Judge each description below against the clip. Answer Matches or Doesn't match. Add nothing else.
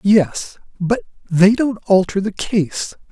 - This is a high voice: Matches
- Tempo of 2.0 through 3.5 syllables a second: Matches